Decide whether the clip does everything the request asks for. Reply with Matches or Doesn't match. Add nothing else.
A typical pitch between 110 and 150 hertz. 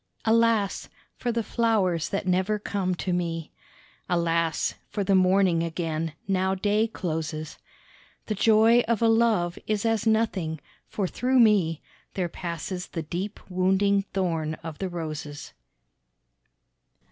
Doesn't match